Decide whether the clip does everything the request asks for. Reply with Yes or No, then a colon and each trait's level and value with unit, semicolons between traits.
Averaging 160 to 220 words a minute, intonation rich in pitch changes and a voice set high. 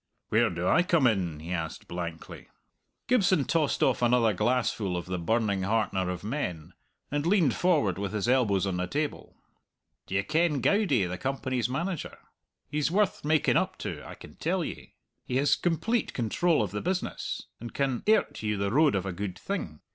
No: average, 180 wpm; wide, 8.0 semitones; low, 120 Hz